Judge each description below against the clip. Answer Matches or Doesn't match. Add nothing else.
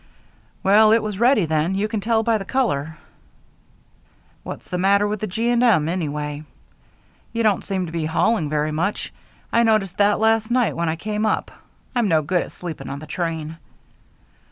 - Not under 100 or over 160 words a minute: Doesn't match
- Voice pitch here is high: Matches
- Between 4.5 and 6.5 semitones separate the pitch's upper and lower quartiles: Matches